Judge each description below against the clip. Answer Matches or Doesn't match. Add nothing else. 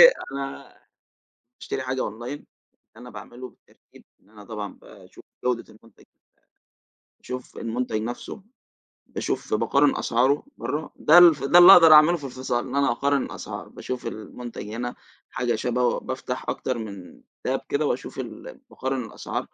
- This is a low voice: Matches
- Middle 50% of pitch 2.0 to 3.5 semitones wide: Matches